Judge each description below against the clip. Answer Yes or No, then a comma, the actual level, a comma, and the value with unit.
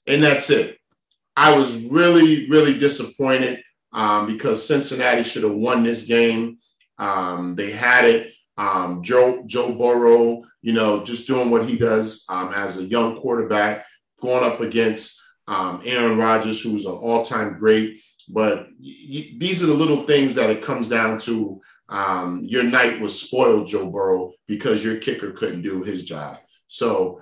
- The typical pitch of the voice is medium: No, low, 115 Hz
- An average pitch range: Yes, average, 3.2 semitones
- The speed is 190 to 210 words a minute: No, average, 160 wpm